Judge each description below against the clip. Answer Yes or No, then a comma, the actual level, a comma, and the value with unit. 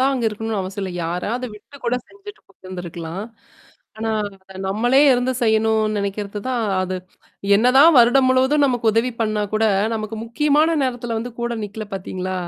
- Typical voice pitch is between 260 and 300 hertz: No, high, 225 Hz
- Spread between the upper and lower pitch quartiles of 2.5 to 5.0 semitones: Yes, average, 4.0 semitones